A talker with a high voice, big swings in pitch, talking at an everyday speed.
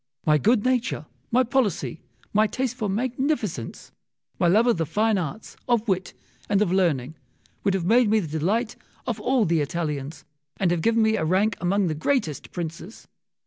Yes: high, 200 Hz; wide, 5.7 semitones; average, 180 wpm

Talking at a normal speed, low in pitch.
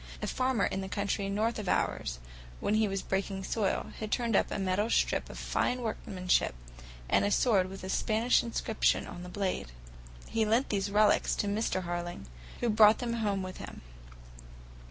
No: average, 180 wpm; high, 205 Hz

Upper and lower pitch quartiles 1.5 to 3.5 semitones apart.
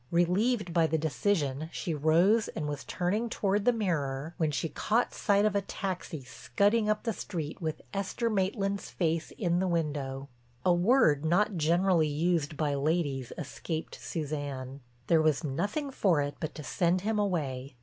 No: average, 5.1 semitones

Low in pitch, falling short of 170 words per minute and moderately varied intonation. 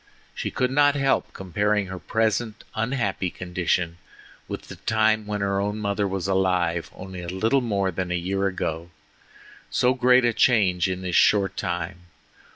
Yes: low, 100 Hz; average, 160 wpm; average, 3.4 semitones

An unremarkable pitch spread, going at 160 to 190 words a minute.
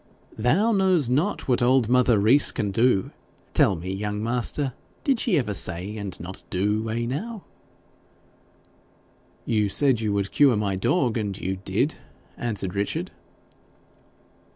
No: average, 4.9 semitones; average, 140 wpm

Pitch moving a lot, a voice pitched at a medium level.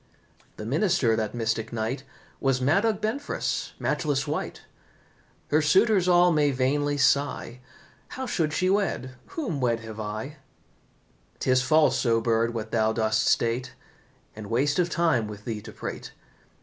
No: wide, 6.0 semitones; low, 130 Hz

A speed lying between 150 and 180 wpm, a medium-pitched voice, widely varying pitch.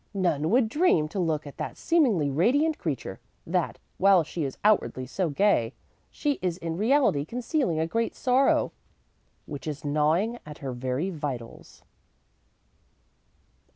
No: average, 140 wpm; medium, 170 Hz; wide, 7.8 semitones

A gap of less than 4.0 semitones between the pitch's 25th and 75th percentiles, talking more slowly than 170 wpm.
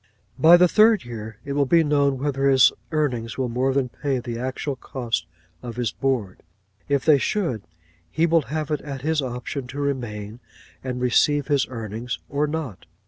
No: average, 3.3 semitones; average, 180 wpm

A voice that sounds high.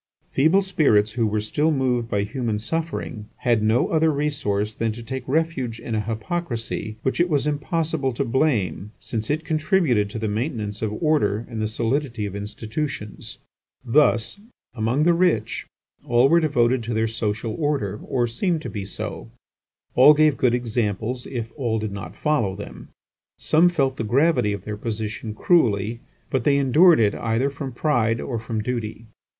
No: low, 120 Hz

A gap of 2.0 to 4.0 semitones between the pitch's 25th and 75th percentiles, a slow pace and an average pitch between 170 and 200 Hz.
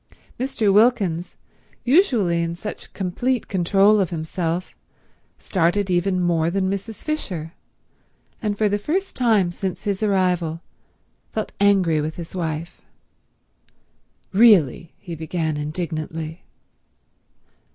Yes: average, 3.7 semitones; slow, 110 wpm; medium, 185 Hz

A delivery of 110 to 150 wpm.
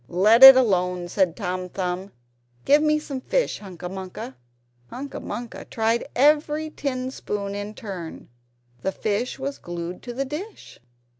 Yes: average, 145 wpm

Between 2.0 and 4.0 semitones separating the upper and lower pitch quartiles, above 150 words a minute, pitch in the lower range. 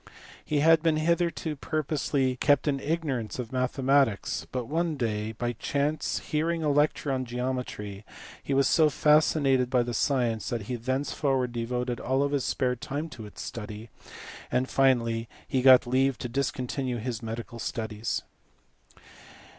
No: average, 3.3 semitones; average, 145 wpm; low, 130 Hz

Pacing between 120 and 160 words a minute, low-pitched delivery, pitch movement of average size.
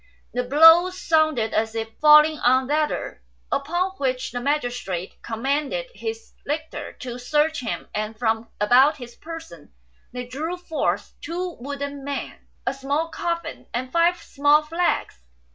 No: average, 145 wpm; very high, 285 Hz; average, 4.7 semitones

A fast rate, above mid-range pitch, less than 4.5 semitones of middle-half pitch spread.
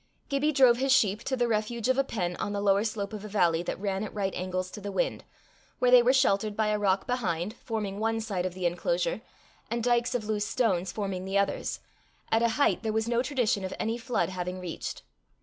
Yes: fast, 230 wpm; high, 215 Hz; average, 3.8 semitones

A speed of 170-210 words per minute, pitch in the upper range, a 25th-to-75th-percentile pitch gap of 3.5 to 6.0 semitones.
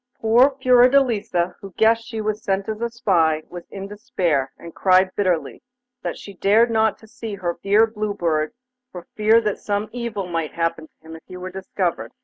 Yes: average, 185 wpm; high, 200 Hz; average, 4.1 semitones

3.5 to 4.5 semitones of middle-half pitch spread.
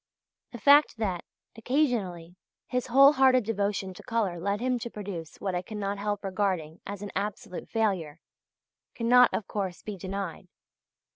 Yes: average, 3.8 semitones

